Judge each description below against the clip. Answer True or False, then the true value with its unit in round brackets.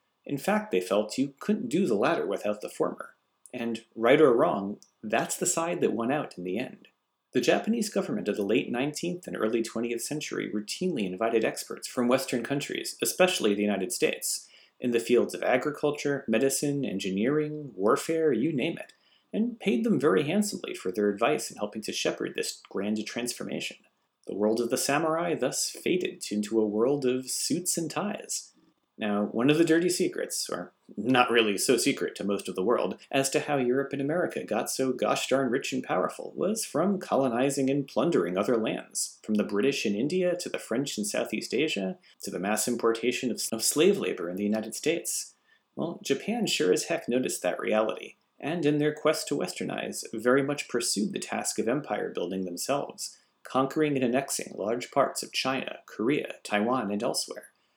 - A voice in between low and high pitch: False (125 Hz)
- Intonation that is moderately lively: False (5.8 semitones)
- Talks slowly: False (185 wpm)